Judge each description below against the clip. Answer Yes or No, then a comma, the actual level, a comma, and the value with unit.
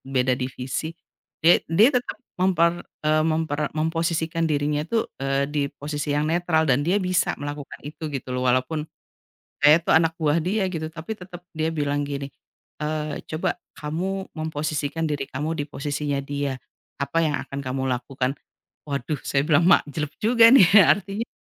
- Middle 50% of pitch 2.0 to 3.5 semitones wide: Yes, average, 2.7 semitones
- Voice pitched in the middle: Yes, medium, 150 Hz